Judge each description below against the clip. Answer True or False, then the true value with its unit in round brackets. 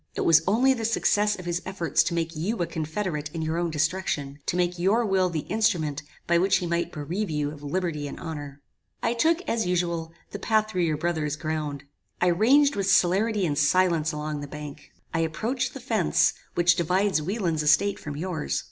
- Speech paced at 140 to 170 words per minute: False (200 wpm)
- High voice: False (170 Hz)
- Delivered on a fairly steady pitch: False (4.2 semitones)